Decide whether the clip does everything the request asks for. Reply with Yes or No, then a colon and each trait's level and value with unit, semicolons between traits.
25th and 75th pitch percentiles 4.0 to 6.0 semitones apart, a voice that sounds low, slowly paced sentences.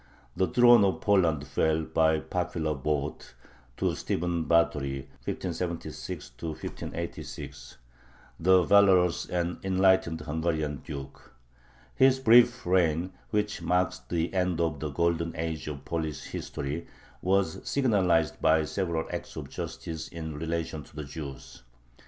No: average, 2.8 semitones; very low, 85 Hz; slow, 120 wpm